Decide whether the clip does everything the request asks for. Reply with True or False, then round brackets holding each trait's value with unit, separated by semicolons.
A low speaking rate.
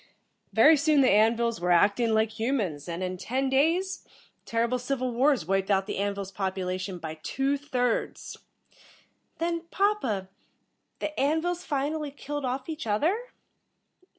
False (150 wpm)